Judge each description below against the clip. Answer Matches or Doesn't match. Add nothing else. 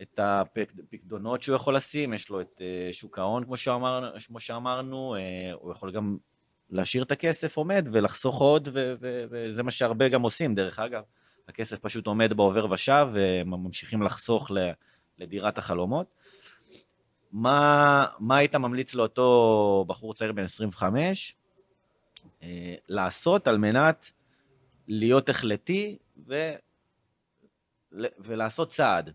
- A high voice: Doesn't match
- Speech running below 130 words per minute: Matches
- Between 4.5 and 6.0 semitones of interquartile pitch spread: Matches